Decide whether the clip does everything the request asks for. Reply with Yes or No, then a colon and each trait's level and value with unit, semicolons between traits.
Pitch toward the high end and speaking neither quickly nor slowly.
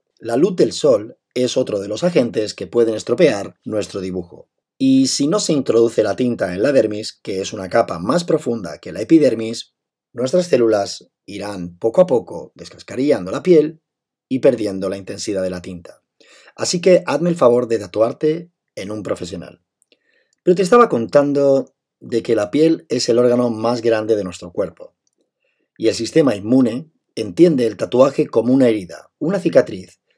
No: low, 120 Hz; average, 175 wpm